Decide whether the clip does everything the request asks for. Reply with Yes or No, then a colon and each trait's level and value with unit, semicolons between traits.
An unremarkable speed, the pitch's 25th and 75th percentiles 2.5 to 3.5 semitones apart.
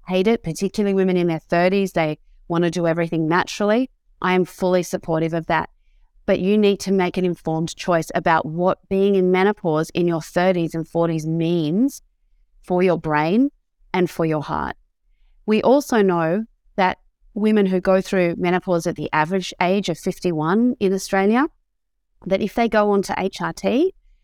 Yes: average, 170 wpm; average, 2.9 semitones